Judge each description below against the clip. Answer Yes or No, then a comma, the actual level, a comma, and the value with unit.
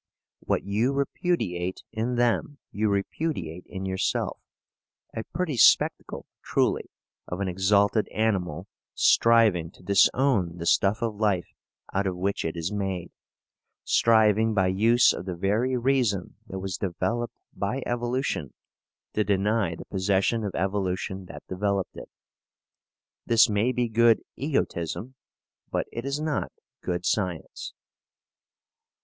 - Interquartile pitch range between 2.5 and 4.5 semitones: Yes, average, 4.0 semitones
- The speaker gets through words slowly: Yes, slow, 130 wpm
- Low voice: Yes, low, 100 Hz